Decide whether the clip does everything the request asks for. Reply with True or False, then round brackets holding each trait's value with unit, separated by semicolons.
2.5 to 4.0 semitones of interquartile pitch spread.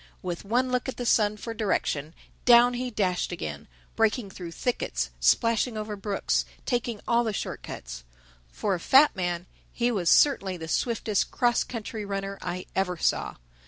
False (4.8 semitones)